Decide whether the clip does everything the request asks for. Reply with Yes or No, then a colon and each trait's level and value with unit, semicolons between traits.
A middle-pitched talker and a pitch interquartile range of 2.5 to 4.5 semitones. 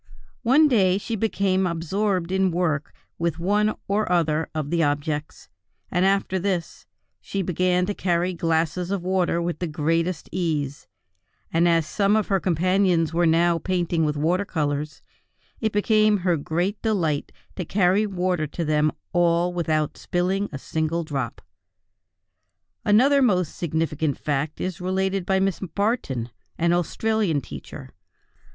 Yes: medium, 175 Hz; average, 3.2 semitones